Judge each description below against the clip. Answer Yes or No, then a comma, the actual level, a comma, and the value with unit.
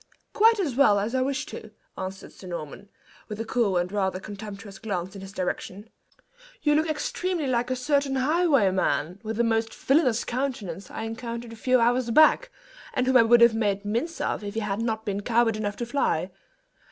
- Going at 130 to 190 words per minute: No, average, 200 wpm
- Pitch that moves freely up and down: No, average, 4.2 semitones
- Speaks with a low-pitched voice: No, high, 225 Hz